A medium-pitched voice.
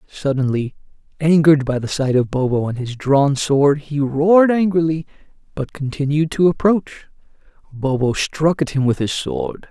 Yes: medium, 145 Hz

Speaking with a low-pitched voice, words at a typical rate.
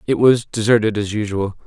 Yes: low, 110 Hz; average, 180 wpm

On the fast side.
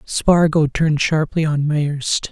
No: slow, 130 wpm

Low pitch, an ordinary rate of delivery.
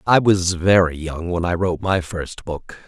No: very low, 90 Hz; fast, 210 wpm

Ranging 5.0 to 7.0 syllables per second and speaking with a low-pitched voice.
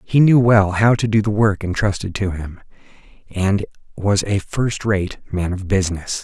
No: 4.4 syllables/s; low, 100 Hz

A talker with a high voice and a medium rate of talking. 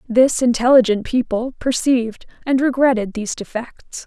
No: high, 240 Hz; slow, 120 wpm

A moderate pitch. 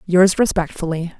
Yes: medium, 180 Hz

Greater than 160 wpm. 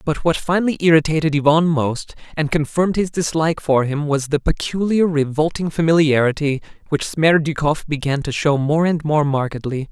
No: average, 155 wpm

